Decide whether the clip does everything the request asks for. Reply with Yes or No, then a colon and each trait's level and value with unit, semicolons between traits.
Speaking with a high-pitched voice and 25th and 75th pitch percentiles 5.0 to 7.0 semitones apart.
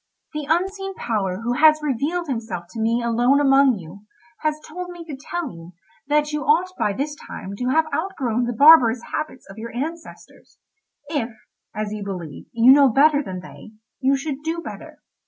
Yes: very high, 270 Hz; wide, 5.4 semitones